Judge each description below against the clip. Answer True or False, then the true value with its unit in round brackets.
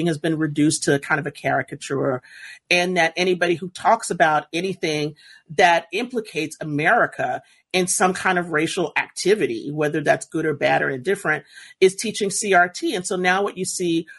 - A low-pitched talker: False (175 Hz)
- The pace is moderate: True (175 wpm)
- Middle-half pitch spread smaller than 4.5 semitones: True (3.3 semitones)